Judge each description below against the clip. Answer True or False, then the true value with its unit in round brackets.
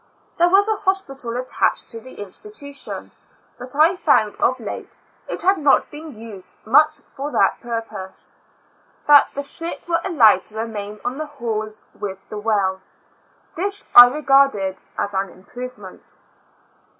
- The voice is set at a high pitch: True (250 Hz)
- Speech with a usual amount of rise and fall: False (6.2 semitones)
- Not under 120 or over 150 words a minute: True (140 wpm)